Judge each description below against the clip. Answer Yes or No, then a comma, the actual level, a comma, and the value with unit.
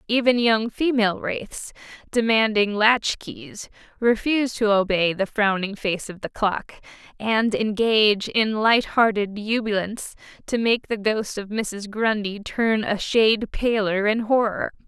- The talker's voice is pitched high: Yes, high, 215 Hz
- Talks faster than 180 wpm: No, slow, 135 wpm